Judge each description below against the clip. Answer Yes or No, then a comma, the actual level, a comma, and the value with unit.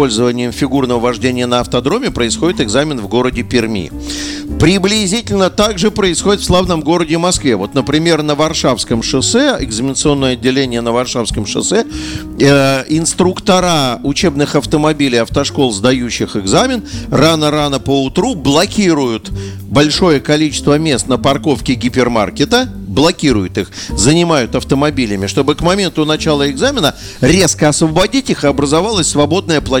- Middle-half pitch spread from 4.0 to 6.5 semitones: Yes, average, 4.6 semitones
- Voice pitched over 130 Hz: Yes, medium, 140 Hz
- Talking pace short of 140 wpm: Yes, average, 120 wpm